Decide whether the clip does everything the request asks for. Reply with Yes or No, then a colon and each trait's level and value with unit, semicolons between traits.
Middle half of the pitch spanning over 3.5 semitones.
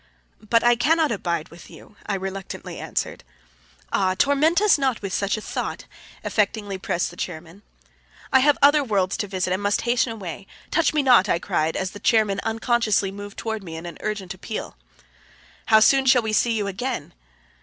Yes: average, 4.1 semitones